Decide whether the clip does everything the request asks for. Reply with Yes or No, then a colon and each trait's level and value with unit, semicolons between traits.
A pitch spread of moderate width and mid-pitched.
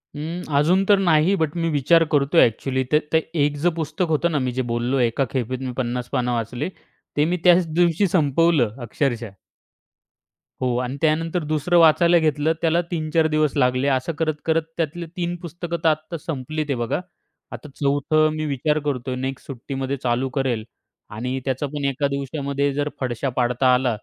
Yes: average, 4.0 semitones; medium, 145 Hz